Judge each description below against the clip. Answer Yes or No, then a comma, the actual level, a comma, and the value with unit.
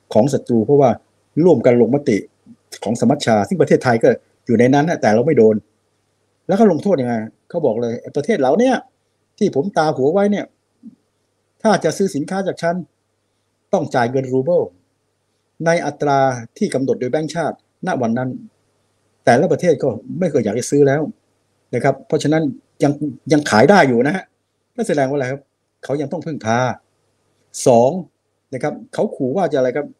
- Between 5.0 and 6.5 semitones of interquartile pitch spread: Yes, wide, 5.6 semitones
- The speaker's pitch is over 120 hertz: Yes, low, 135 Hz